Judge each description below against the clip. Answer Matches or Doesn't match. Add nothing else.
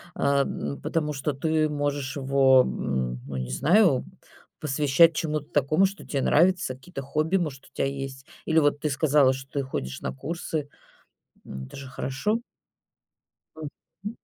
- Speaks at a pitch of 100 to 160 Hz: Matches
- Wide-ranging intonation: Doesn't match